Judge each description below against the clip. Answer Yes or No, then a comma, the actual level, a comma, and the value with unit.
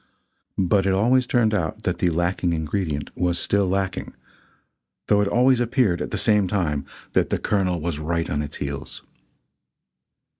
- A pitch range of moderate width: Yes, average, 3.8 semitones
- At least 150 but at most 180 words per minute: Yes, average, 160 wpm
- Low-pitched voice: Yes, very low, 95 Hz